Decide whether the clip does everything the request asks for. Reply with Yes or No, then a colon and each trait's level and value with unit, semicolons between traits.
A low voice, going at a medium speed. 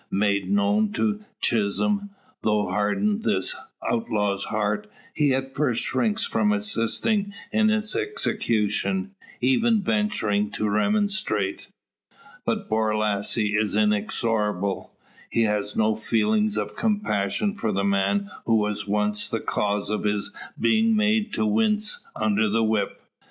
No: low, 110 Hz; slow, 125 wpm